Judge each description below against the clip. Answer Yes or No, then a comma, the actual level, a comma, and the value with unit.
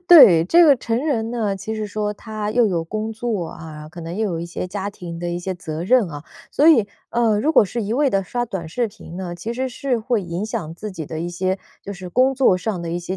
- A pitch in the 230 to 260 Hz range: No, high, 205 Hz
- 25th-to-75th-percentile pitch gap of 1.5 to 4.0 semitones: No, average, 5.0 semitones